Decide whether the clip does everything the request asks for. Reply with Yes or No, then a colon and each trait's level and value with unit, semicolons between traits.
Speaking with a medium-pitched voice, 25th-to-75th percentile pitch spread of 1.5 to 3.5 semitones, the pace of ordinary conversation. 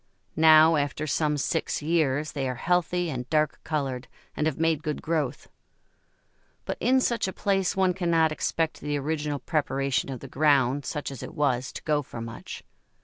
Yes: medium, 150 Hz; average, 2.9 semitones; average, 175 wpm